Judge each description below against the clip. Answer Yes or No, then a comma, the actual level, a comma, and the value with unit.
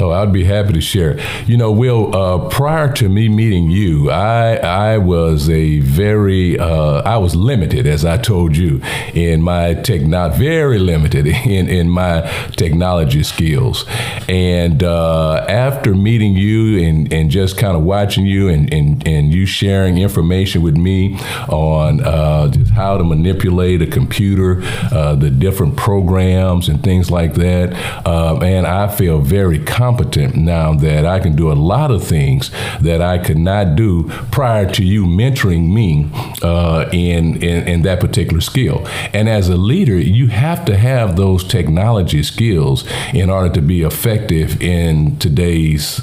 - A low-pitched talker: Yes, very low, 95 Hz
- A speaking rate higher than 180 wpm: No, average, 165 wpm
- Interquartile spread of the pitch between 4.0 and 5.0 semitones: Yes, average, 4.7 semitones